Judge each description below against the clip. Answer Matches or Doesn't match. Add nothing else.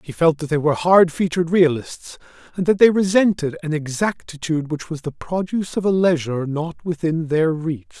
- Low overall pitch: Doesn't match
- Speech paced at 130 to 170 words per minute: Doesn't match